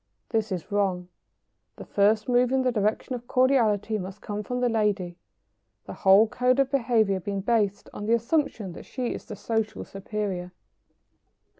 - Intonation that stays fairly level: No, average, 3.5 semitones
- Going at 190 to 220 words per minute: No, average, 165 wpm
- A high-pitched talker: Yes, high, 215 Hz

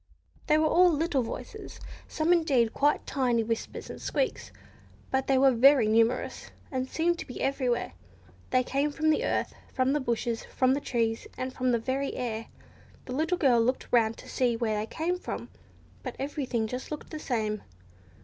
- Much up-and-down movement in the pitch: No, average, 4.0 semitones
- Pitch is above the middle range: Yes, very high, 260 Hz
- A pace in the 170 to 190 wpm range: Yes, average, 180 wpm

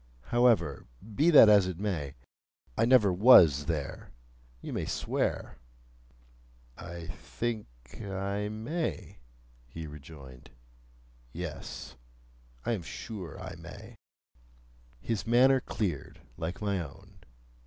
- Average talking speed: No, slow, 105 wpm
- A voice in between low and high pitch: No, very low, 95 Hz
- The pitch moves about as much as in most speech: No, wide, 6.0 semitones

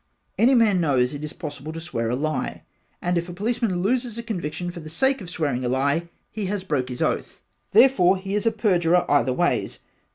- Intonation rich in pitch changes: Yes, wide, 5.8 semitones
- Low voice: No, medium, 175 Hz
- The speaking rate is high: Yes, fast, 215 wpm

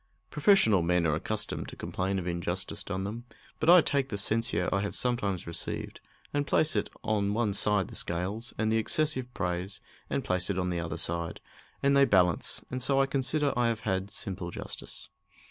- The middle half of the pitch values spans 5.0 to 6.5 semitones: Yes, wide, 5.5 semitones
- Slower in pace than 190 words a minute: No, average, 195 wpm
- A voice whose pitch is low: Yes, low, 100 Hz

